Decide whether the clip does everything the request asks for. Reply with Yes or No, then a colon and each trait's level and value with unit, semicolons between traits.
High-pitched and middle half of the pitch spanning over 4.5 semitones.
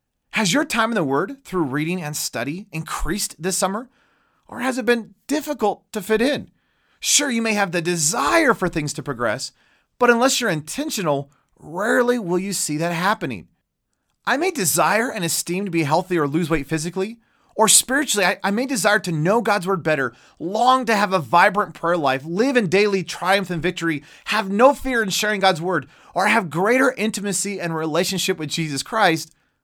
Yes: high, 195 Hz; wide, 5.5 semitones